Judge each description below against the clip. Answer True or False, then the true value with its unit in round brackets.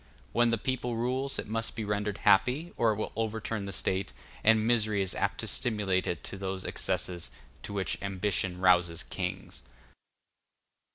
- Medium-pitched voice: False (105 Hz)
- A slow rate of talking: False (165 wpm)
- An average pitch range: True (3.2 semitones)